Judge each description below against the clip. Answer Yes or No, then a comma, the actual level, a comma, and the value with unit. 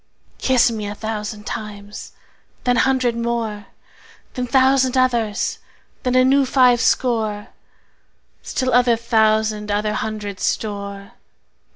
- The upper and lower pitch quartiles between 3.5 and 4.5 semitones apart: No, average, 3.1 semitones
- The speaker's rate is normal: No, slow, 110 wpm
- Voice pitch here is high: Yes, high, 225 Hz